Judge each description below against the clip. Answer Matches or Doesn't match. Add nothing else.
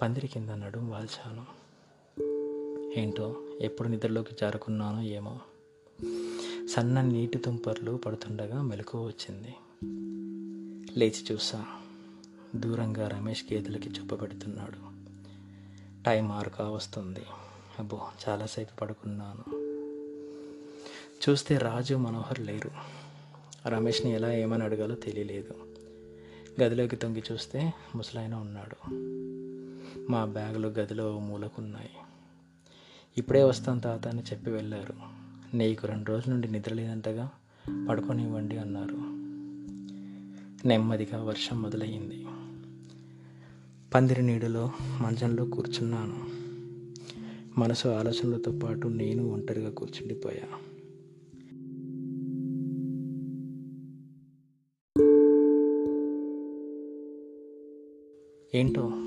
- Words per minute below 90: Matches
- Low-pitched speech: Matches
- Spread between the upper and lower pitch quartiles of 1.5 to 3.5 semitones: Doesn't match